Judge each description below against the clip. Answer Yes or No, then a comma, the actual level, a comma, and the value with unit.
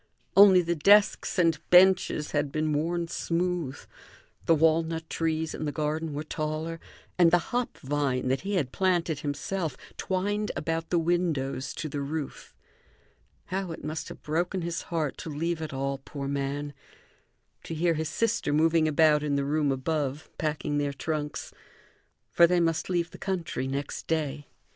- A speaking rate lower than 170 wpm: Yes, average, 160 wpm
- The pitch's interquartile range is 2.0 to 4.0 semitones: Yes, average, 2.8 semitones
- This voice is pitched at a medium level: Yes, medium, 160 Hz